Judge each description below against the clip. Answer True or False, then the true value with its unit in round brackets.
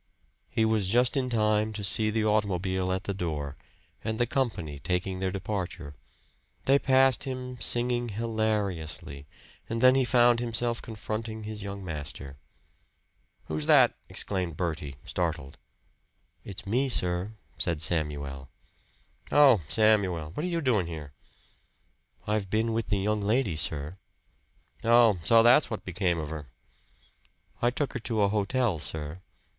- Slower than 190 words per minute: True (140 wpm)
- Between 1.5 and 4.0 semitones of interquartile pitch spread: False (5.2 semitones)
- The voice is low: True (105 Hz)